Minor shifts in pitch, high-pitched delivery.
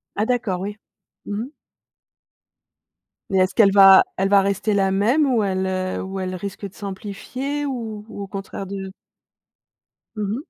Yes: narrow, 2.1 semitones; high, 200 Hz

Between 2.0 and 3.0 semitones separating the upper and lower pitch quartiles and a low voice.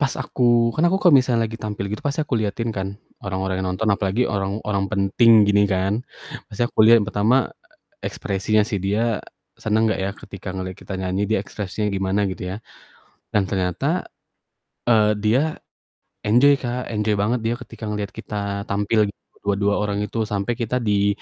Yes: average, 2.7 semitones; low, 105 Hz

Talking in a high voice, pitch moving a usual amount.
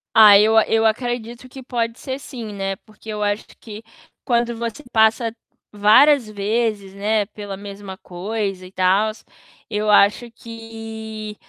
No: high, 220 Hz; narrow, 2.1 semitones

